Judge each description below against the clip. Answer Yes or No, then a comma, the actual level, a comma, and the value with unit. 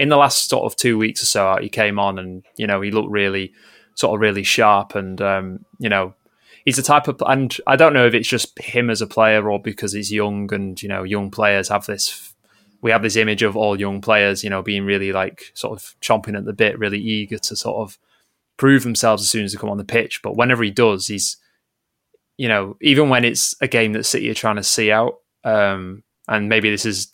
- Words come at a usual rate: No, fast, 245 wpm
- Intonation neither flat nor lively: No, narrow, 2.3 semitones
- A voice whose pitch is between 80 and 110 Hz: Yes, low, 105 Hz